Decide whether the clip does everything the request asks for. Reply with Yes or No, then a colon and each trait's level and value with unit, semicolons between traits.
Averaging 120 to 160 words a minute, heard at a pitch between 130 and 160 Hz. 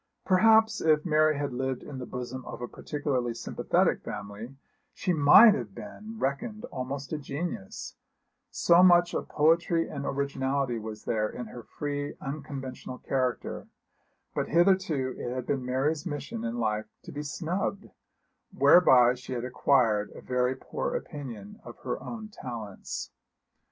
Yes: average, 145 wpm; low, 135 Hz